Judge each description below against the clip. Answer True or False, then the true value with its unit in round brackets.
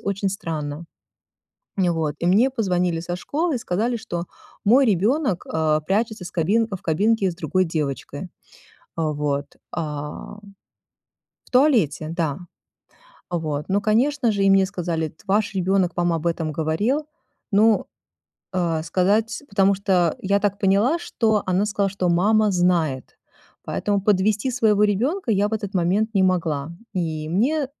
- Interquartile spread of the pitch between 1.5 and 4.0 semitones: False (4.4 semitones)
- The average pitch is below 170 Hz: False (190 Hz)